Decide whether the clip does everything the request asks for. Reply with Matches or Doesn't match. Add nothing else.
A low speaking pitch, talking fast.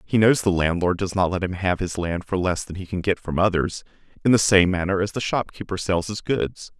Matches